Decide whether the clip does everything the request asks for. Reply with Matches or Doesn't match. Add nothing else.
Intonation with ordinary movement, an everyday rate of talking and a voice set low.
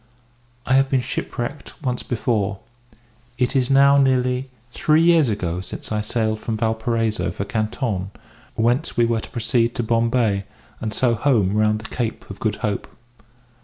Matches